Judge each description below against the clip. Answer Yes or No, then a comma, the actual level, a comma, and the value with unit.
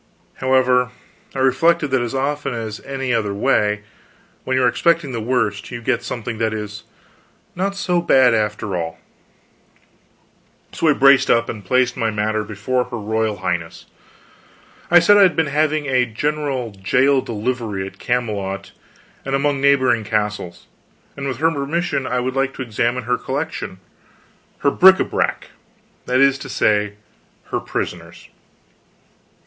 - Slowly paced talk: No, average, 155 wpm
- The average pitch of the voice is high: No, low, 125 Hz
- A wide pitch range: No, average, 4.3 semitones